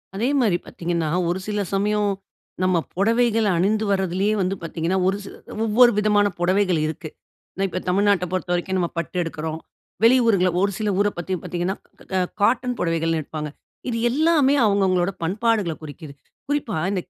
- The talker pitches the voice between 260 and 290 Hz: No, high, 195 Hz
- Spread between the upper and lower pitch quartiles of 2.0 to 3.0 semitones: No, average, 3.5 semitones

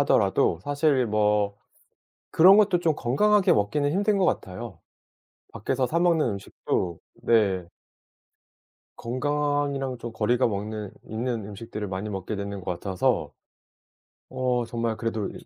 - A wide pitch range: Yes, wide, 5.7 semitones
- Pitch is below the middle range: Yes, low, 115 Hz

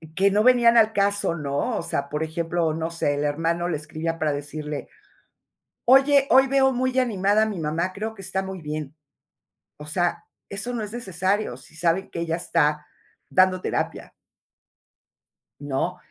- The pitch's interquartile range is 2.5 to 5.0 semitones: No, wide, 5.4 semitones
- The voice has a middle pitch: Yes, medium, 175 Hz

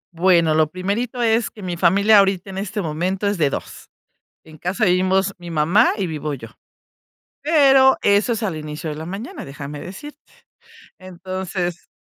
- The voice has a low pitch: No, medium, 185 Hz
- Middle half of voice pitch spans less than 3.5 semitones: No, average, 3.9 semitones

